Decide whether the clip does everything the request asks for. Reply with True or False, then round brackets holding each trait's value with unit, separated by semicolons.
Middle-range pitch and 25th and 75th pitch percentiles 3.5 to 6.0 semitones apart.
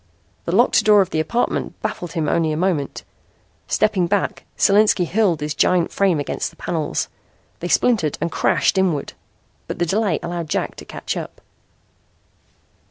True (175 Hz; 3.9 semitones)